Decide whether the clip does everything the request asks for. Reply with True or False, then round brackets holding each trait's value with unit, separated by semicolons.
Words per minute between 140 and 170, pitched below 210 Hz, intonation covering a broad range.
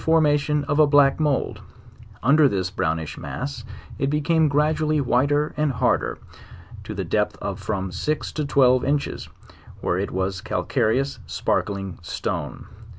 True (150 wpm; 140 Hz; 5.9 semitones)